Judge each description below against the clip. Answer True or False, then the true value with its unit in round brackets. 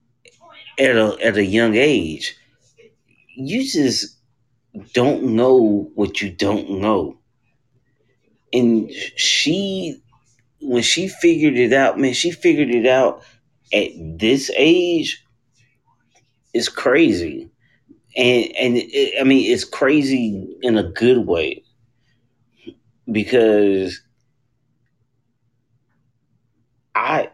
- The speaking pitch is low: True (125 Hz)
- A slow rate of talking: True (95 wpm)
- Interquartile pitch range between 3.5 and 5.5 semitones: True (4.1 semitones)